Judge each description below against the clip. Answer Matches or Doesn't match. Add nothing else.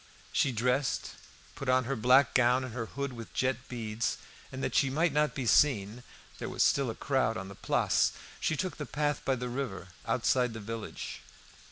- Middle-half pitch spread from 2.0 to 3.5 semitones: Matches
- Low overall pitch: Matches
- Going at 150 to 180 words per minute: Doesn't match